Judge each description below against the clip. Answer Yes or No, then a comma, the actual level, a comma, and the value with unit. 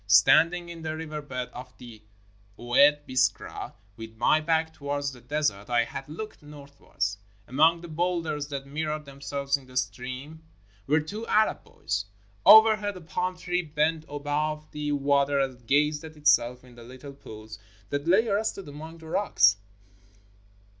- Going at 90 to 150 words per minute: No, average, 160 wpm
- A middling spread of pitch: Yes, average, 3.8 semitones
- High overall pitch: No, medium, 145 Hz